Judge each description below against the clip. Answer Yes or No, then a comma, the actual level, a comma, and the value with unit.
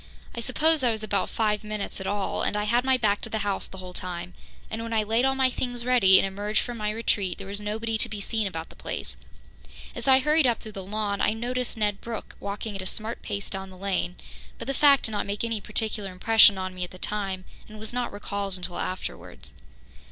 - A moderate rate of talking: No, fast, 245 wpm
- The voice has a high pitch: Yes, high, 210 Hz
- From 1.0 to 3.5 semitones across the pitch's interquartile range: Yes, average, 2.9 semitones